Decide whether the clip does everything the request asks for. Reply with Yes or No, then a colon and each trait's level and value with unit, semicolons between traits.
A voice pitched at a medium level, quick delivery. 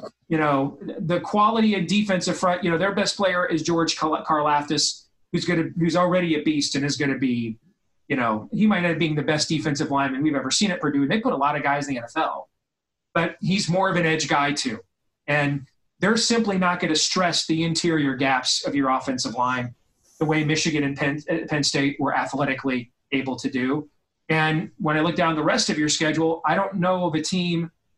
Yes: medium, 155 Hz; fast, 220 wpm